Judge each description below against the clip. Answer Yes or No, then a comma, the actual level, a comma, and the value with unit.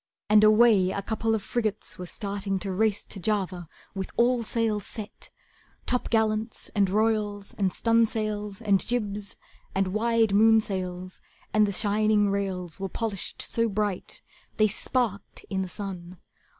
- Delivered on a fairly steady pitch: Yes, narrow, 2.2 semitones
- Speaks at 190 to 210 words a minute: No, average, 140 wpm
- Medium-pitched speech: No, high, 210 Hz